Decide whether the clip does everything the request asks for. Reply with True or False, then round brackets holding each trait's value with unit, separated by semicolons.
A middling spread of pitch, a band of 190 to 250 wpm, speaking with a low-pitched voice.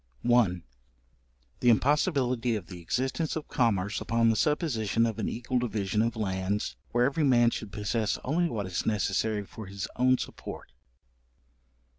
False (3.7 semitones; 155 wpm; 115 Hz)